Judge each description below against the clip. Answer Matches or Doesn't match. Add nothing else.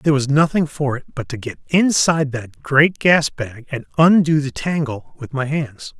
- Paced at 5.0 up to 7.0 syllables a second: Doesn't match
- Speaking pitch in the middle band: Matches